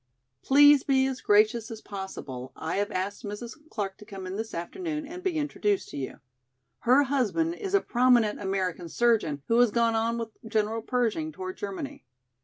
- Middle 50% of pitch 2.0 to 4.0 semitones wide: No, average, 5.3 semitones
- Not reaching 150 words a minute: No, average, 180 wpm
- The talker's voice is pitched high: Yes, high, 225 Hz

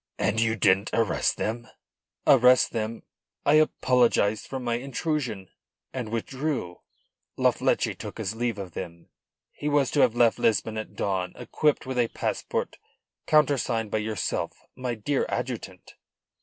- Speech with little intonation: No, average, 3.4 semitones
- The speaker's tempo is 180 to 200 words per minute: No, average, 140 wpm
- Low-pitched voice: Yes, low, 115 Hz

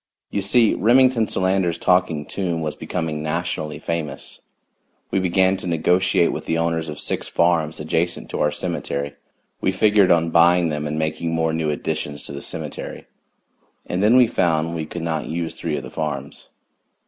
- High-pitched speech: No, very low, 85 Hz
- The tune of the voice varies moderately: Yes, average, 3.0 semitones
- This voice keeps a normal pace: Yes, average, 170 wpm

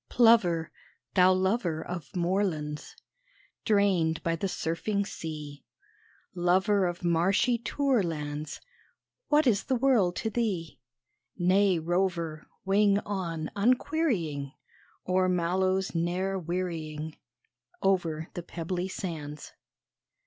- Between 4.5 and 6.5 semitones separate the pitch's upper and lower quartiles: No, average, 3.4 semitones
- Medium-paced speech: No, slow, 100 wpm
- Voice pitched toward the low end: No, medium, 180 Hz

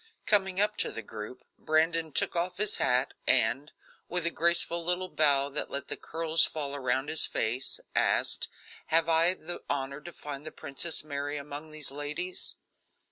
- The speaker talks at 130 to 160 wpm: No, average, 170 wpm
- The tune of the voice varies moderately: Yes, average, 3.5 semitones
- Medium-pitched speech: Yes, medium, 155 Hz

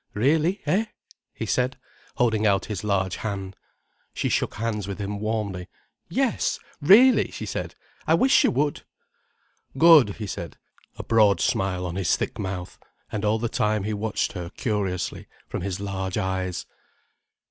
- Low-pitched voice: Yes, low, 105 Hz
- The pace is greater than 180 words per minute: No, average, 155 wpm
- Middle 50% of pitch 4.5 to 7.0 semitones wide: No, average, 3.1 semitones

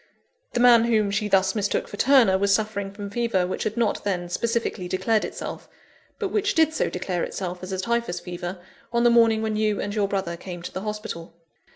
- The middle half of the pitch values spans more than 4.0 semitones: No, average, 3.5 semitones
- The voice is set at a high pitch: Yes, high, 205 Hz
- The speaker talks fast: Yes, fast, 210 wpm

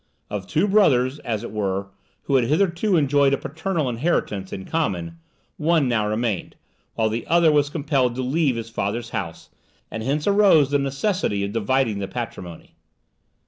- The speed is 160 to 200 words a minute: Yes, average, 165 wpm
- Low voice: Yes, low, 130 Hz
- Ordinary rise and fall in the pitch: No, wide, 6.2 semitones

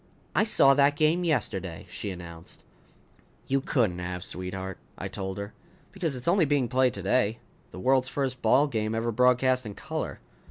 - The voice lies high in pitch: No, low, 125 Hz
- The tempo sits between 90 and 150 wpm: No, average, 165 wpm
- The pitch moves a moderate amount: No, wide, 6.1 semitones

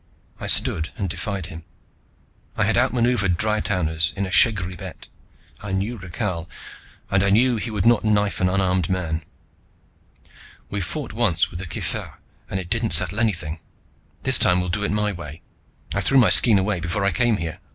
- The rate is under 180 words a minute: No, average, 185 wpm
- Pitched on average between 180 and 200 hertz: No, very low, 95 Hz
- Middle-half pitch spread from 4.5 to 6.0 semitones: No, average, 3.4 semitones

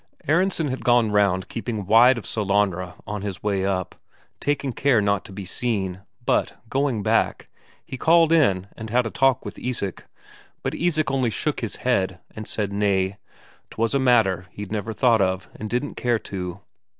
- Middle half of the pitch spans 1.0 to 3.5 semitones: No, average, 4.6 semitones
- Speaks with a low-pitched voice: Yes, low, 110 Hz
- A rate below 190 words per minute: Yes, average, 175 wpm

